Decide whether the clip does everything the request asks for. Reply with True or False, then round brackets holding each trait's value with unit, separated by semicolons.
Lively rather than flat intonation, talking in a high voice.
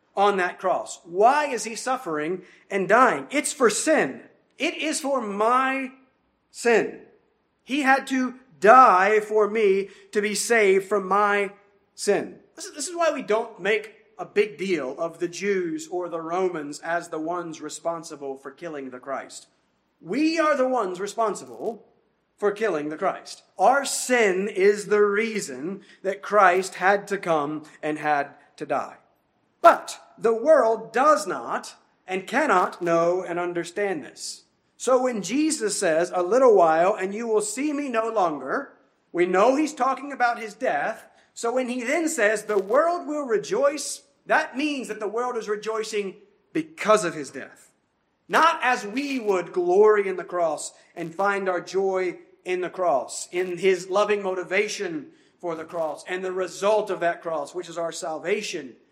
True (6.2 semitones; 205 Hz)